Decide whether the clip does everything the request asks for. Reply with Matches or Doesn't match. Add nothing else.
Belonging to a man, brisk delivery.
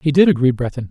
Matches